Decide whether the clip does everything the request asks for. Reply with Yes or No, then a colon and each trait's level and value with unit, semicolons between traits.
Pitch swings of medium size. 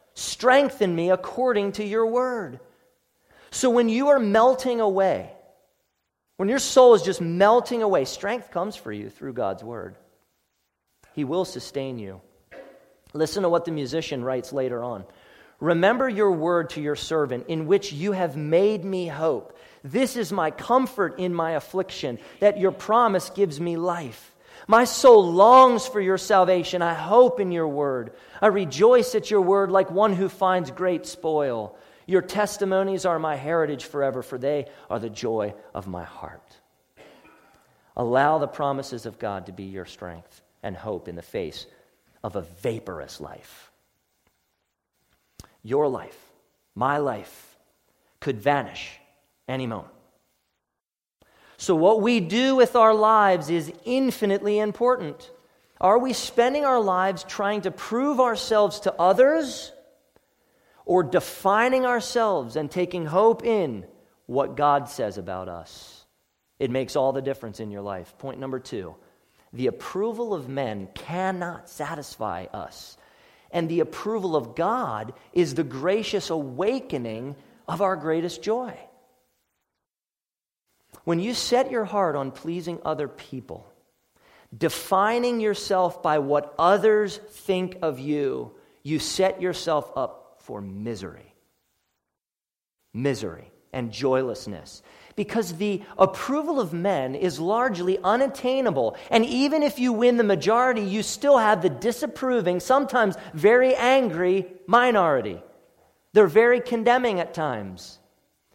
No: wide, 7.7 semitones